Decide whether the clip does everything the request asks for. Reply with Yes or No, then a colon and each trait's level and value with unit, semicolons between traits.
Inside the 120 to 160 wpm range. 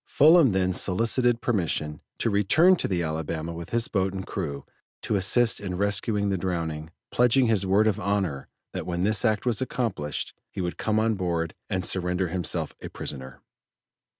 No: average, 175 wpm